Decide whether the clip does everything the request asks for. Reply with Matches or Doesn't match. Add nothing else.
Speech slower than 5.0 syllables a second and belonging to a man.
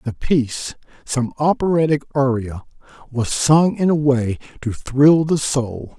Matches